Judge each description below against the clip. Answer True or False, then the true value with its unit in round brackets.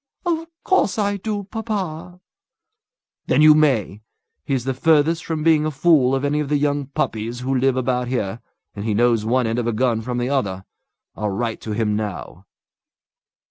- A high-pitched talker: False (130 Hz)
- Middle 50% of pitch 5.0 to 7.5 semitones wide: True (5.4 semitones)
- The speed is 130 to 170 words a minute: False (180 wpm)